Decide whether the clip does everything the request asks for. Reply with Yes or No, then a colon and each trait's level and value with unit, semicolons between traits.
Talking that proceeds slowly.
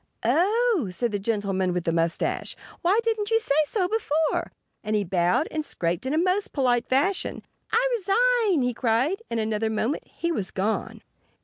No: average, 175 wpm